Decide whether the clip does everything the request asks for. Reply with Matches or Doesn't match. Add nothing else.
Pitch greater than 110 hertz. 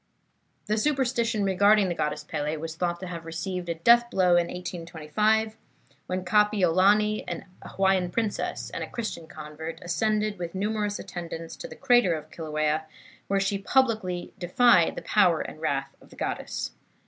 Matches